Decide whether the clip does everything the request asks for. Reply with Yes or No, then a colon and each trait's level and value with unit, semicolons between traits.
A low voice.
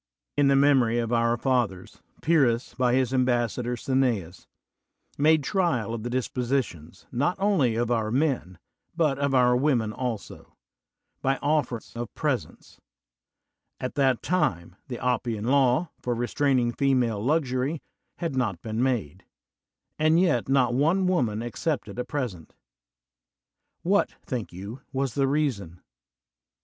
Yes: low, 125 Hz